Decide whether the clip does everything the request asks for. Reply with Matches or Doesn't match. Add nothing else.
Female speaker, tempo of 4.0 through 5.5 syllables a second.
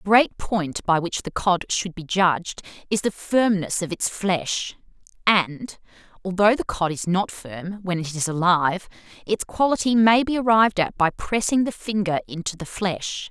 Matches